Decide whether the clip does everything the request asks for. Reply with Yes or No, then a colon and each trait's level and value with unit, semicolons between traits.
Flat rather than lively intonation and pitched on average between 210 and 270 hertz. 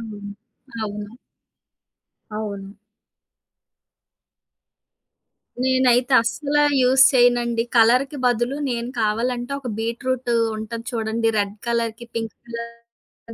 Yes: narrow, 1.9 semitones; high, 235 Hz